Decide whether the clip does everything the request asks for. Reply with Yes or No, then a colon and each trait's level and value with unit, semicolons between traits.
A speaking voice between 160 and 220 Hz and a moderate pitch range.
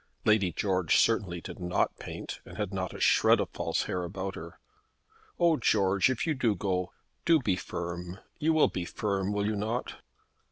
No: low, 100 Hz; average, 3.4 semitones